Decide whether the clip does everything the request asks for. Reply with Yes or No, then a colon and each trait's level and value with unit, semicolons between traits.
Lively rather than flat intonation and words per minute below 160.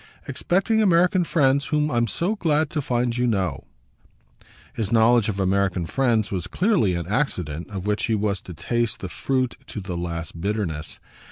No: wide, 7.0 semitones; average, 170 wpm